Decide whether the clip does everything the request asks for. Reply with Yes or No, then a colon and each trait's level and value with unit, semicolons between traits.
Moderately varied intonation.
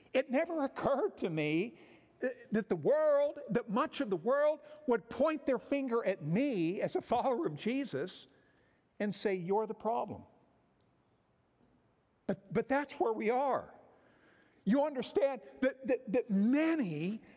No: wide, 5.7 semitones